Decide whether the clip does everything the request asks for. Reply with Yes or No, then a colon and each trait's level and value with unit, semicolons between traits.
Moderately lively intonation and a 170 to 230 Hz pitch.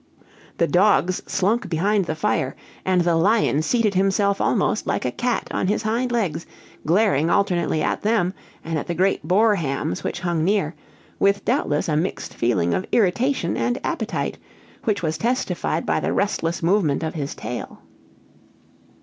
Yes: average, 4.7 semitones; medium, 185 Hz